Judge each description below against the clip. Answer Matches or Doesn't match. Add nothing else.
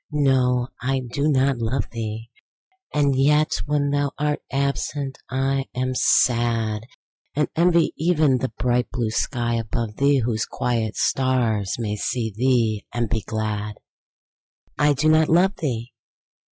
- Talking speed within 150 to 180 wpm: Doesn't match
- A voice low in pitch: Matches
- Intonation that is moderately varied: Matches